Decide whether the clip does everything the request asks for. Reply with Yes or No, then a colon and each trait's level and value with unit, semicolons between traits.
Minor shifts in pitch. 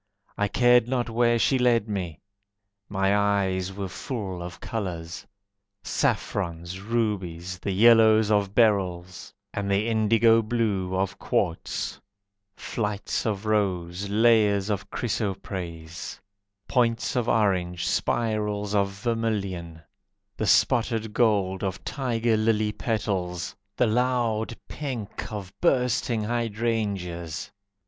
No: average, 3.3 semitones